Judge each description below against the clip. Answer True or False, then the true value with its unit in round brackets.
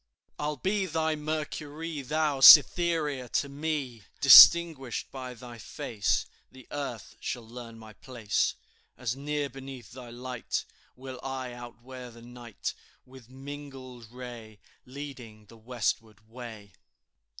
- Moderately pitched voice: False (130 Hz)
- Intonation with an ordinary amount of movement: True (3.4 semitones)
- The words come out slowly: True (120 wpm)